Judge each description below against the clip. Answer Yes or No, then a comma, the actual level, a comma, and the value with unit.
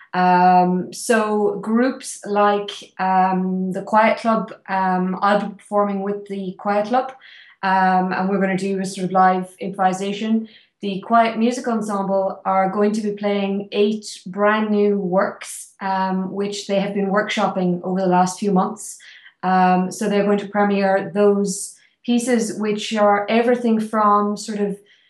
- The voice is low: No, high, 200 Hz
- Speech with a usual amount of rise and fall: No, narrow, 1.8 semitones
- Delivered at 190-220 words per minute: No, average, 155 wpm